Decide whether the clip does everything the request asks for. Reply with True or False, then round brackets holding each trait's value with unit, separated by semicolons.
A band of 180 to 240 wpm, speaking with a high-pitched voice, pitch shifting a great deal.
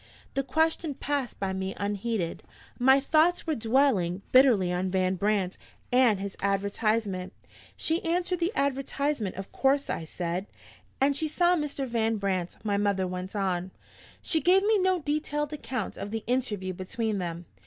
False (155 wpm; 225 Hz; 7.0 semitones)